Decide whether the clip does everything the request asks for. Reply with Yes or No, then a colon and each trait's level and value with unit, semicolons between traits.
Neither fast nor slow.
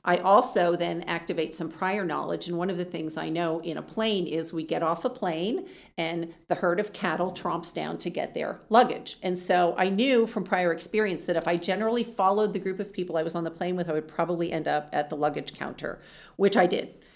No: fast, 240 wpm